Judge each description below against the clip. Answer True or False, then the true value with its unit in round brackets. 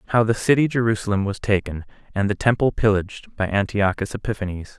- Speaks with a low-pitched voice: True (105 Hz)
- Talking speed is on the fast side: False (165 wpm)